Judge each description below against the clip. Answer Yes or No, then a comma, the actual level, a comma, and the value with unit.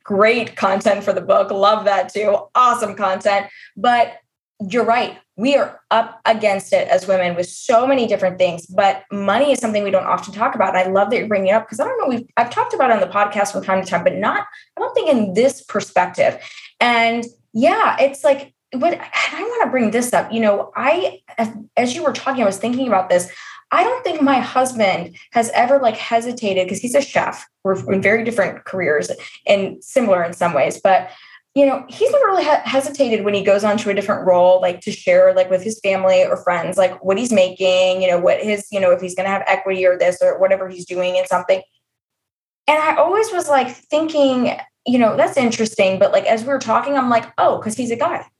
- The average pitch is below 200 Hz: No, high, 220 Hz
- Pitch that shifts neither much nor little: No, wide, 5.8 semitones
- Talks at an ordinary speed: No, fast, 225 wpm